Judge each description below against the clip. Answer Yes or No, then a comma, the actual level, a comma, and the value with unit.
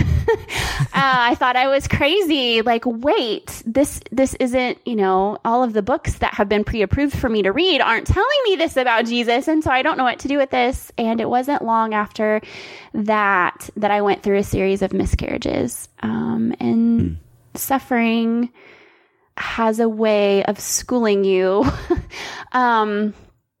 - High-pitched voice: Yes, high, 230 Hz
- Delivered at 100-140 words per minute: No, average, 170 wpm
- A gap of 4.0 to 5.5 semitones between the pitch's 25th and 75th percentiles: Yes, average, 4.4 semitones